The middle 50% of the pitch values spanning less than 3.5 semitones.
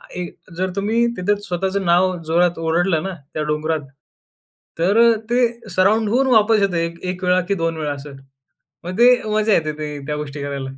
No: average, 4.0 semitones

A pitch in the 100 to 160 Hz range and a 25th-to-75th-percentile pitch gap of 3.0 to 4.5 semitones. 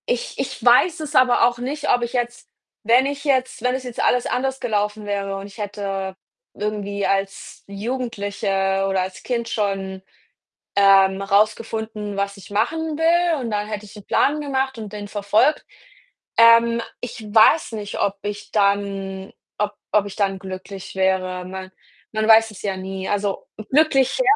No: high, 210 Hz; average, 3.7 semitones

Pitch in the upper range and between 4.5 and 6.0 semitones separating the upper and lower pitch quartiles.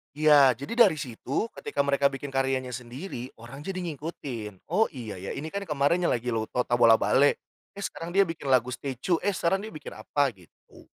No: medium, 140 Hz; average, 5.1 semitones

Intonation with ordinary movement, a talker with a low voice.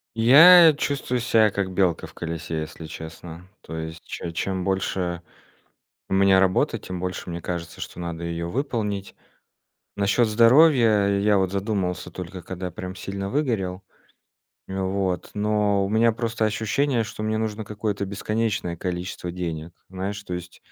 Yes: average, 3.6 semitones; very low, 95 Hz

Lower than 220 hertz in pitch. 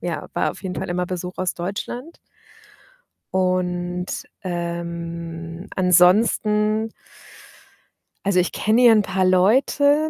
Yes: medium, 185 Hz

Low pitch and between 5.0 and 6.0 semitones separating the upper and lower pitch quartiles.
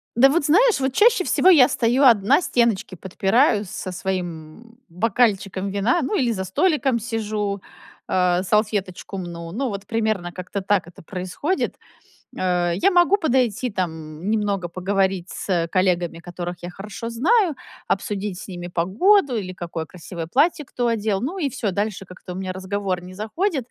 No: high, 200 Hz; average, 5.3 semitones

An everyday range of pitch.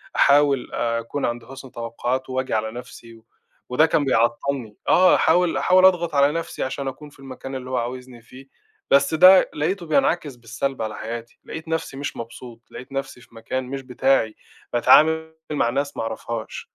Yes: average, 3.7 semitones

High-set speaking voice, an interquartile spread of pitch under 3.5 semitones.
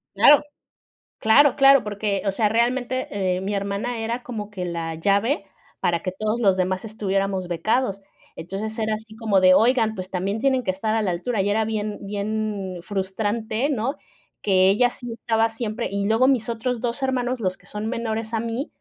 Yes: high, 215 Hz; average, 3.1 semitones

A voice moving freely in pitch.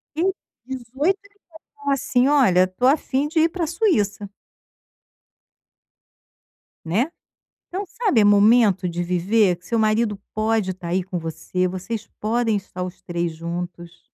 Yes: wide, 6.6 semitones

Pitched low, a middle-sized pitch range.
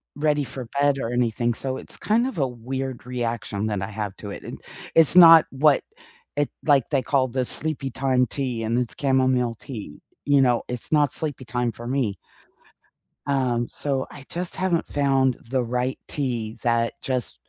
Yes: low, 130 Hz; average, 3.0 semitones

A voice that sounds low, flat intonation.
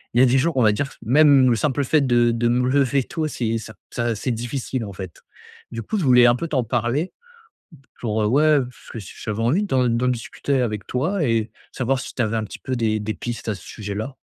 No: low, 120 Hz; average, 3.1 semitones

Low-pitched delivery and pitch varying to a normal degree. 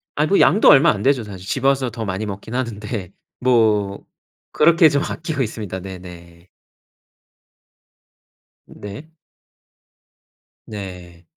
No: low, 110 Hz; wide, 5.9 semitones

